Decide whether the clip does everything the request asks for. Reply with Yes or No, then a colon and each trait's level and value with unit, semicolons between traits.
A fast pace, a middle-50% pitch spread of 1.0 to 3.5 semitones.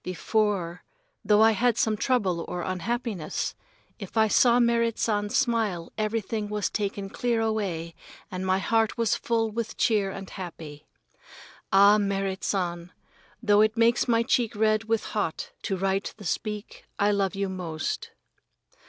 No: average, 150 wpm; average, 2.9 semitones